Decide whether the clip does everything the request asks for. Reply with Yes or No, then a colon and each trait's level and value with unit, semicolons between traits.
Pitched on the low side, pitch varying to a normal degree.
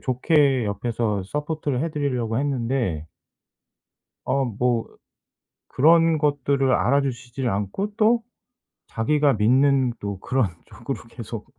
Yes: low, 130 Hz; average, 4.0 semitones